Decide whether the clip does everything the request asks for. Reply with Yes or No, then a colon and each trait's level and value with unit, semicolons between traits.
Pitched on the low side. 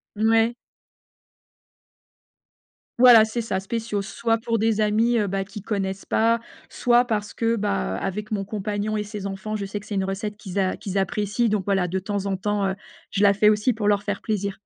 No: high, 210 Hz